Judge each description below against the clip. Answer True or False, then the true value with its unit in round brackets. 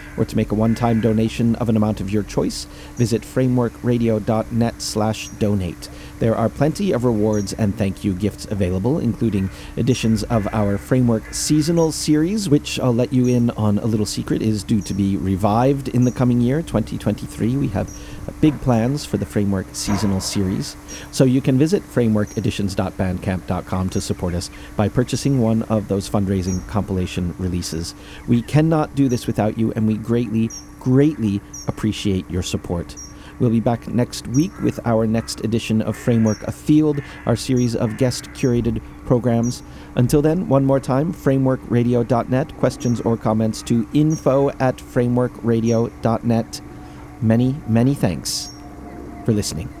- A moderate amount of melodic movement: True (3.6 semitones)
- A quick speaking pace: False (155 wpm)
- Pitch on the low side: True (115 Hz)